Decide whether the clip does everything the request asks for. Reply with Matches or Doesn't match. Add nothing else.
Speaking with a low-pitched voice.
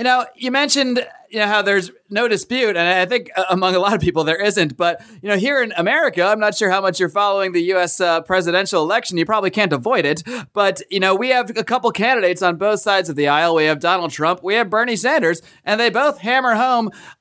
Doesn't match